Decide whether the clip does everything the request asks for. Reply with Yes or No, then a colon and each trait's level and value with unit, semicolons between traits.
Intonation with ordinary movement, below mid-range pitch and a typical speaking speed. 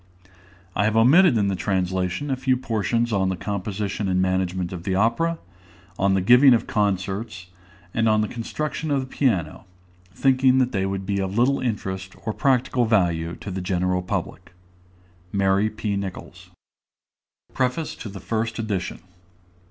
Yes: average, 4.3 semitones; low, 100 Hz; average, 160 wpm